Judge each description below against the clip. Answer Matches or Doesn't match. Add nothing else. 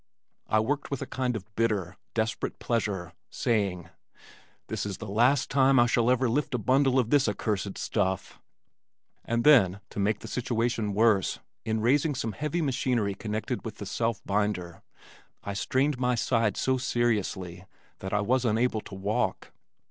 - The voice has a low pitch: Matches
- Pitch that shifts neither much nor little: Matches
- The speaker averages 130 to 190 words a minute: Matches